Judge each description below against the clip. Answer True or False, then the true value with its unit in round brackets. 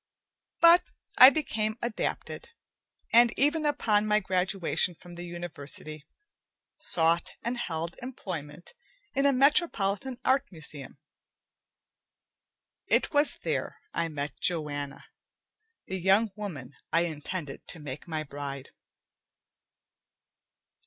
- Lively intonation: True (7.4 semitones)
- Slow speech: True (105 wpm)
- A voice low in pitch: False (180 Hz)